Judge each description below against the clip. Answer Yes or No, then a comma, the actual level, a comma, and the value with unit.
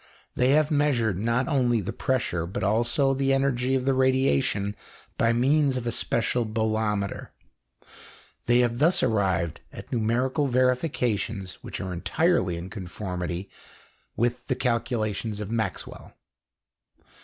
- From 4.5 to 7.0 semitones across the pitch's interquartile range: No, average, 4.1 semitones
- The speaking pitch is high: No, low, 120 Hz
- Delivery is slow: Yes, slow, 130 wpm